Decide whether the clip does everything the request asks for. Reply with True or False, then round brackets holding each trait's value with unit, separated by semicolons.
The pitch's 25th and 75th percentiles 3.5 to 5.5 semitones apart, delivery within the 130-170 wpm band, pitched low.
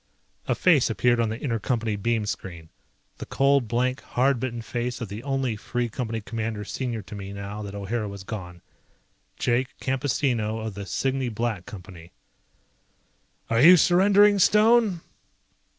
True (4.2 semitones; 150 wpm; 115 Hz)